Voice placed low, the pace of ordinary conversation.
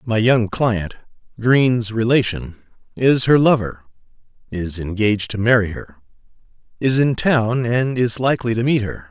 No: low, 115 Hz; slow, 130 wpm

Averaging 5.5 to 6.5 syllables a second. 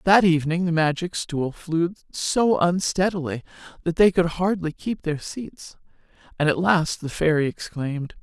No: 4.5 syllables/s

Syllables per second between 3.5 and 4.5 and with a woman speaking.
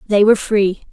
No: 5.3 syllables/s; female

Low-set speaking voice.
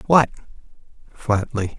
Yes: low, 120 Hz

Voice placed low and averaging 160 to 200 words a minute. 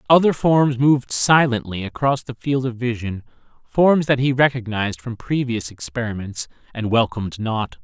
No: low, 120 Hz; average, 145 wpm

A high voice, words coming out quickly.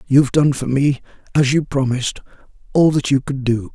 No: low, 135 Hz; fast, 210 wpm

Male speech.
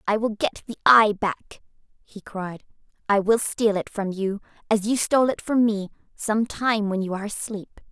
No: female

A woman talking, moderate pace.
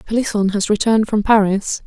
Yes: female; average, 160 wpm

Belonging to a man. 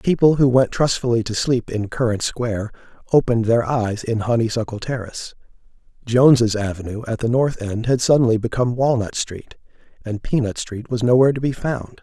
Yes: male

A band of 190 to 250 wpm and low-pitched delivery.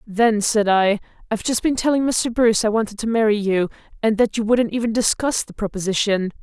No: fast, 205 wpm; high, 220 Hz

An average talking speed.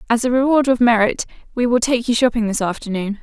No: fast, 225 wpm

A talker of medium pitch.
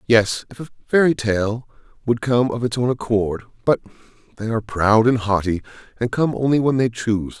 No: low, 115 Hz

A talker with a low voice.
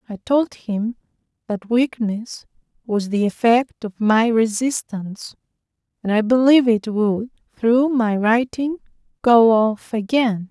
No: high, 230 Hz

